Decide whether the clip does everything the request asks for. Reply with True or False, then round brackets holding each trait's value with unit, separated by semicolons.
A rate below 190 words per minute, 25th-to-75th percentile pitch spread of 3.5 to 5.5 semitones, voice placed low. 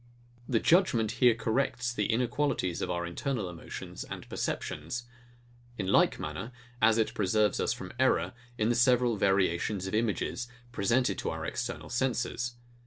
True (150 wpm; 4.1 semitones; 115 Hz)